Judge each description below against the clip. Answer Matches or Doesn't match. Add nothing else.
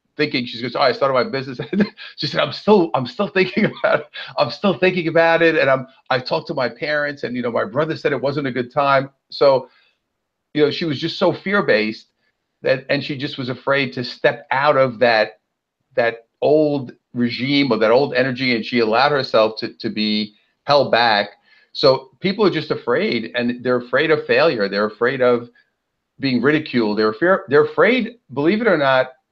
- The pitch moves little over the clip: Doesn't match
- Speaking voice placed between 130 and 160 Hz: Matches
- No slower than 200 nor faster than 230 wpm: Matches